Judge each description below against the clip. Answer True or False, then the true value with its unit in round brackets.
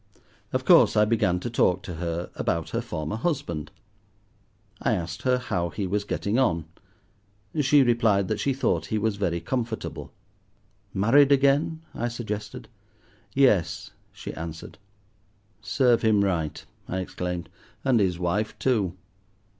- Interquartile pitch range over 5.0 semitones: True (5.5 semitones)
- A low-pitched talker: True (105 Hz)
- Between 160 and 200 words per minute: False (140 wpm)